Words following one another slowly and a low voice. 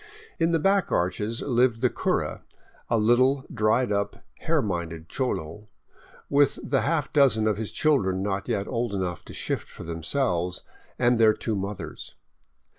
No: average, 155 wpm; low, 110 Hz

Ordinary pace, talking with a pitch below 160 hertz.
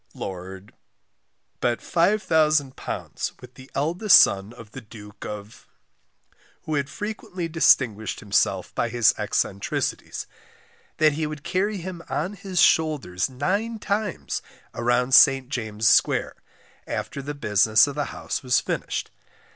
No: slow, 125 wpm; low, 135 Hz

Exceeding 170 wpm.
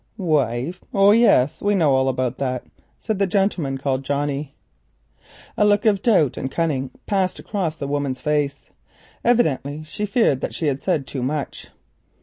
No: average, 160 wpm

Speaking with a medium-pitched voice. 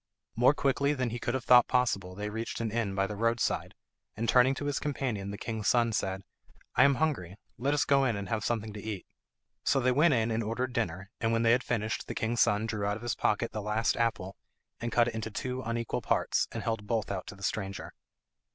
No: low, 115 Hz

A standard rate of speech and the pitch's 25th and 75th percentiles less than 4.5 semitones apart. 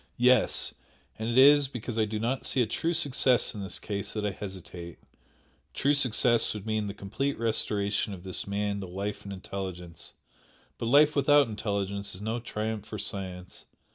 Yes: average, 175 wpm; average, 3.7 semitones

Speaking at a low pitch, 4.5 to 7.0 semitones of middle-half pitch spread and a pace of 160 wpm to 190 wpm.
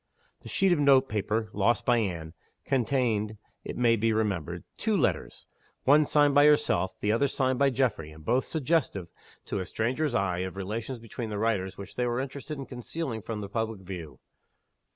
Yes: low, 115 Hz; average, 5.3 semitones; average, 185 wpm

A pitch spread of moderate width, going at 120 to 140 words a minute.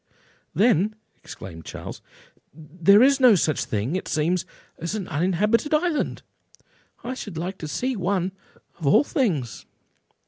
No: wide, 6.4 semitones; slow, 135 wpm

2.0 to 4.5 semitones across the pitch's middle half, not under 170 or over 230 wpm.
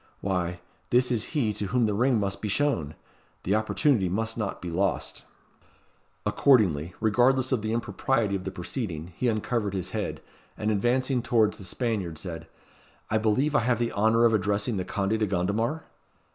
Yes: average, 3.8 semitones; average, 175 wpm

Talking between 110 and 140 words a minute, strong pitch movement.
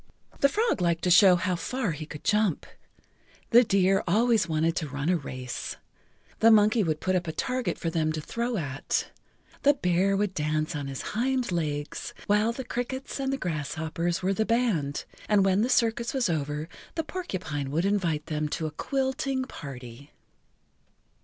No: average, 180 wpm; wide, 7.0 semitones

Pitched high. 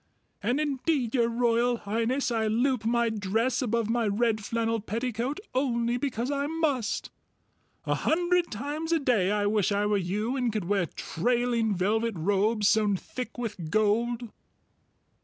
Yes: high, 230 Hz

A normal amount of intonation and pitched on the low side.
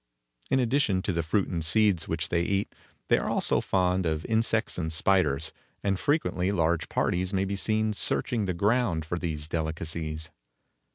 Yes: average, 4.0 semitones; very low, 90 Hz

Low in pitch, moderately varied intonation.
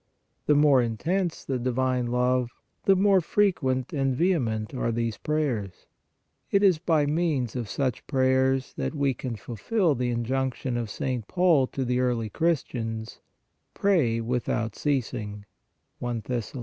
Yes: low, 130 Hz; average, 4.3 semitones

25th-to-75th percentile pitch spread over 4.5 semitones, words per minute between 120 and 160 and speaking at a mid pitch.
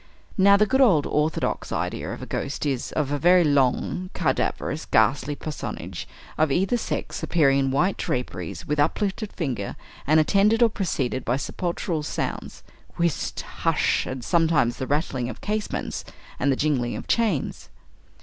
Yes: average, 5.3 semitones; average, 155 wpm; medium, 150 Hz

